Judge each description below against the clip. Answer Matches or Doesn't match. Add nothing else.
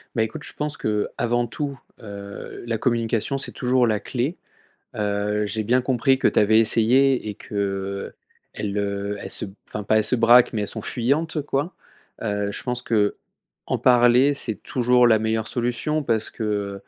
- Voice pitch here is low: Matches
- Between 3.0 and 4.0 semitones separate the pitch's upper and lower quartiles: Matches